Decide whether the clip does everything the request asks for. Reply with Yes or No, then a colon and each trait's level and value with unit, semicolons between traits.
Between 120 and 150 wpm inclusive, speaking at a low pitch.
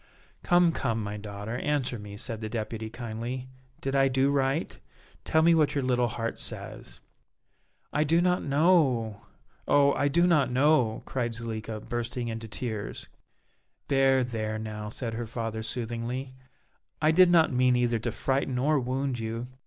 No: average, 160 wpm; low, 125 Hz